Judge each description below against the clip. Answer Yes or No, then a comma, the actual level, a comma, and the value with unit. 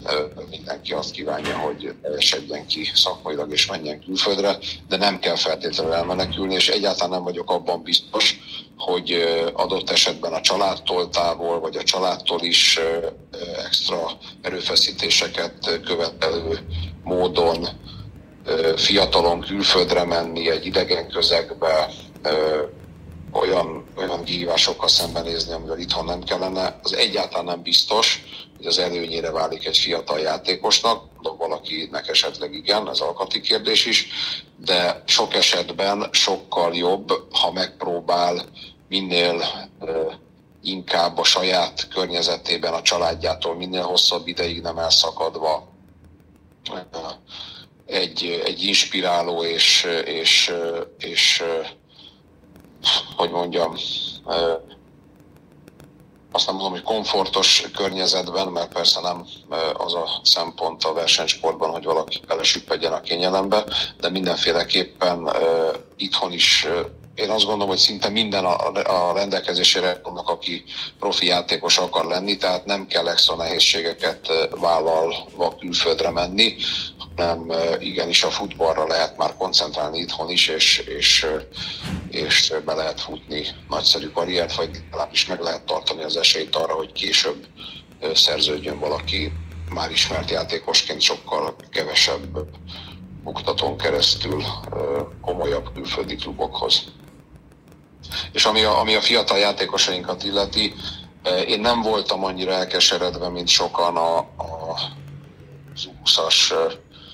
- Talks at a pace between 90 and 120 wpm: Yes, average, 115 wpm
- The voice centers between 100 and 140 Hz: No, very low, 90 Hz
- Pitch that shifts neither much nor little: No, narrow, 2.3 semitones